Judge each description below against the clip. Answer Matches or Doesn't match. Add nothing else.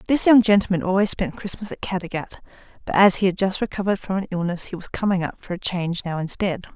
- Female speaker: Matches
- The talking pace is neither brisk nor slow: Doesn't match